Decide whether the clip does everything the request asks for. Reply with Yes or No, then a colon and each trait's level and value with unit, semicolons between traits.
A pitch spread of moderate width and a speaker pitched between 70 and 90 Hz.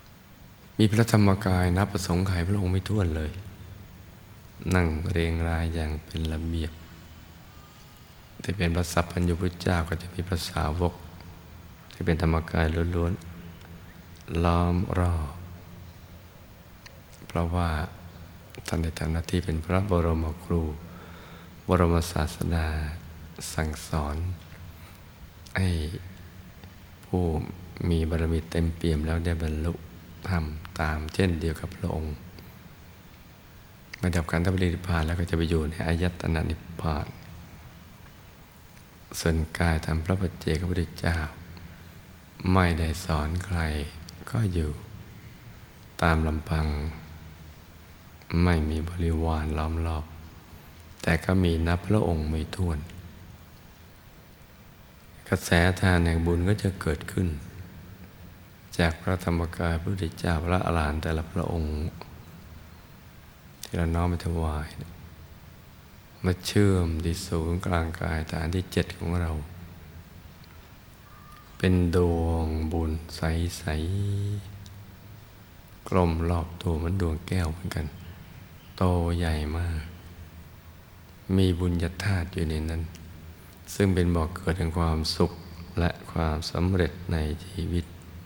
No: narrow, 1.9 semitones; very low, 85 Hz